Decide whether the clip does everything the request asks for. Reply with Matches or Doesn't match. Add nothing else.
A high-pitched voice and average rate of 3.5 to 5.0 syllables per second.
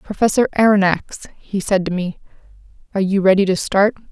Doesn't match